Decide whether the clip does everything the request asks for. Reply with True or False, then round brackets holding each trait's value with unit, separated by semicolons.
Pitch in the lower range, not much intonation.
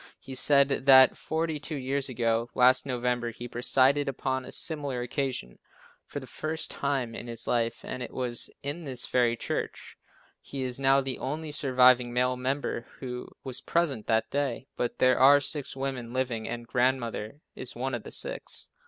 True (130 Hz; 2.2 semitones)